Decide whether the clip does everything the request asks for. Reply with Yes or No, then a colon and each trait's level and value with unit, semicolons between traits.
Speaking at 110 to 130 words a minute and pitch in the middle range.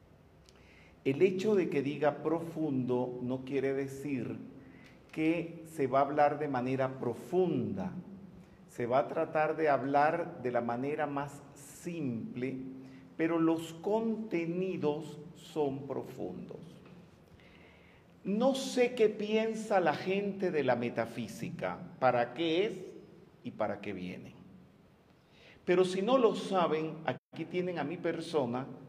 Yes: slow, 125 wpm; medium, 155 Hz